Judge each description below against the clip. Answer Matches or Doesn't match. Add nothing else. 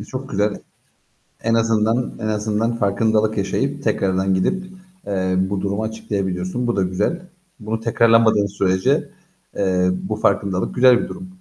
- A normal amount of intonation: Matches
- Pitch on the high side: Doesn't match